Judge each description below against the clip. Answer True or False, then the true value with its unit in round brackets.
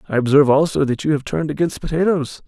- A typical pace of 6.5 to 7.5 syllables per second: True (7.1 syllables/s)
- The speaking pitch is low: False (150 Hz)